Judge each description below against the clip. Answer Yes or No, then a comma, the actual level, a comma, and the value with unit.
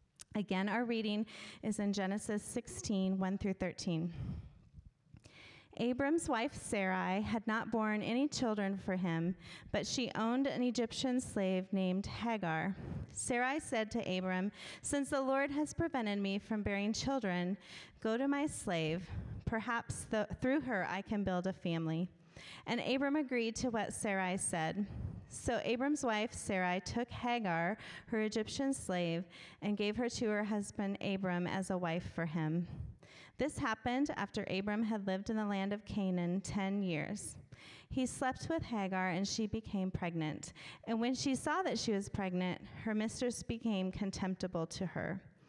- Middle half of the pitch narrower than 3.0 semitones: No, average, 3.9 semitones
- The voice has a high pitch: Yes, high, 205 Hz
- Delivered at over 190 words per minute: No, average, 150 wpm